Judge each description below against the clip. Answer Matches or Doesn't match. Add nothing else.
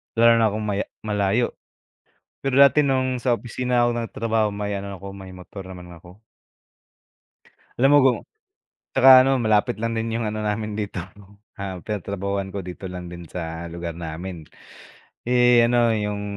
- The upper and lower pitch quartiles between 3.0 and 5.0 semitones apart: Matches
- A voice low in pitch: Matches